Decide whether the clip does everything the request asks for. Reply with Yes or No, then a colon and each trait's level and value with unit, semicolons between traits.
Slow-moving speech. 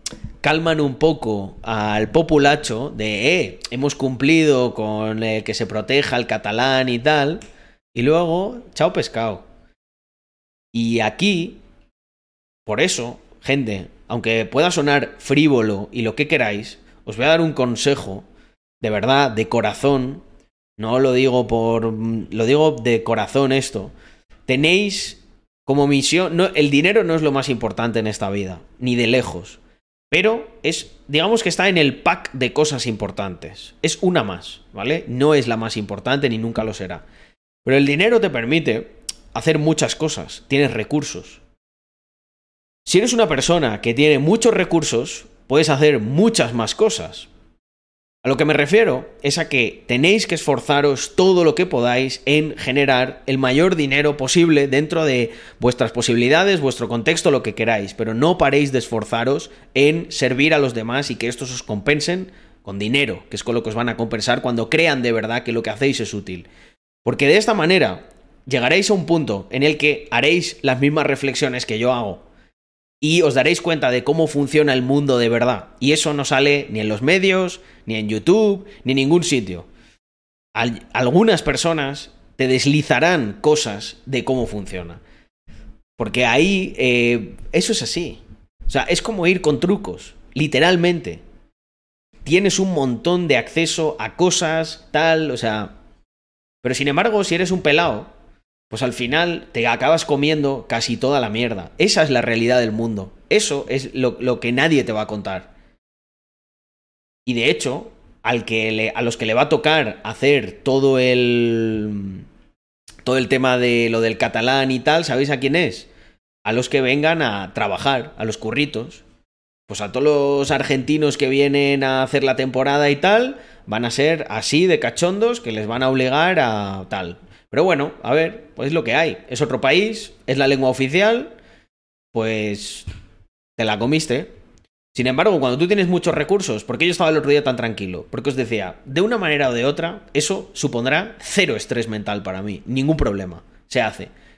No: average, 170 wpm